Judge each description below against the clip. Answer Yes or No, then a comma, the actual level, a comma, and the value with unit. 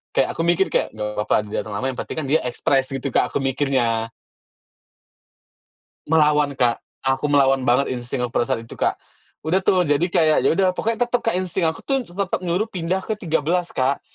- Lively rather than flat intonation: Yes, wide, 5.7 semitones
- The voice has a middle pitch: Yes, medium, 145 Hz